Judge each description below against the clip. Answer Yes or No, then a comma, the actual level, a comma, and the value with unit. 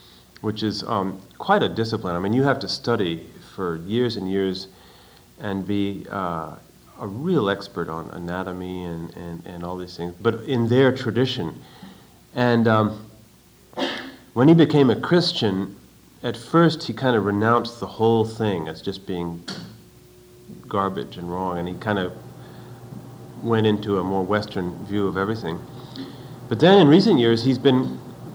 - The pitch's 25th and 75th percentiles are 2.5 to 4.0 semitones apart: No, average, 4.5 semitones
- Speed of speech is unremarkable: Yes, average, 160 wpm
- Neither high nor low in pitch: No, low, 105 Hz